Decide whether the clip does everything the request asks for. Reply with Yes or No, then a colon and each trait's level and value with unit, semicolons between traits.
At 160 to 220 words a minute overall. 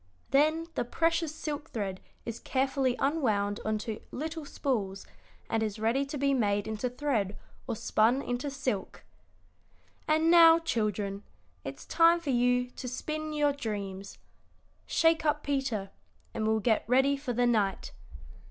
No: average, 145 wpm